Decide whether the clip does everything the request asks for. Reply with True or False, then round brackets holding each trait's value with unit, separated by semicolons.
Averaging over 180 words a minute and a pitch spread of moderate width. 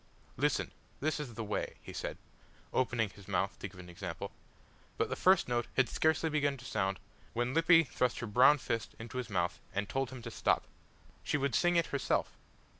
False (195 wpm; 5.9 semitones)